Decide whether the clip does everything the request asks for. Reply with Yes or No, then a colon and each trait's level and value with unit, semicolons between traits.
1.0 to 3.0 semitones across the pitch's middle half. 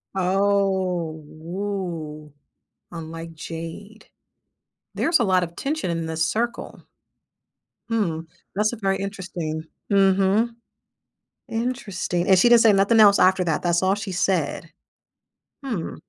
No: average, 3.5 semitones